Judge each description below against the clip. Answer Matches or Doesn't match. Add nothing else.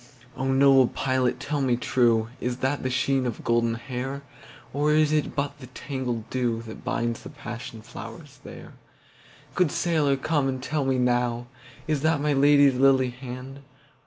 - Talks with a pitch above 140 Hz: Doesn't match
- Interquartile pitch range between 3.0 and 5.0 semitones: Doesn't match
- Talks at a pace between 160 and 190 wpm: Doesn't match